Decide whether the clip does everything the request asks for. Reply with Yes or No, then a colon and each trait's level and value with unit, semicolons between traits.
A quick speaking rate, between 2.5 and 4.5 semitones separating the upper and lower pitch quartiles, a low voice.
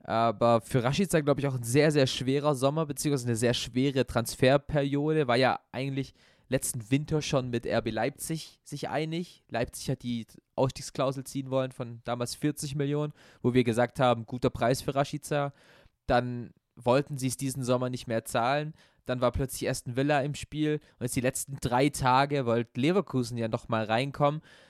No: average, 175 wpm; average, 2.9 semitones; low, 130 Hz